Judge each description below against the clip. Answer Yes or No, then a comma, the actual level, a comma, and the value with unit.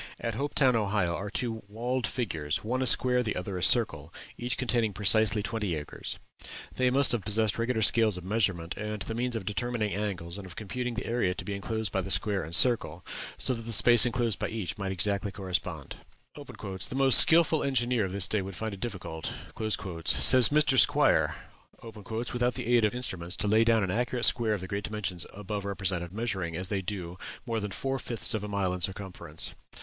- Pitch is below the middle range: Yes, low, 105 Hz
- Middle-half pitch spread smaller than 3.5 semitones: No, average, 3.8 semitones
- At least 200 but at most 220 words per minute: Yes, fast, 205 wpm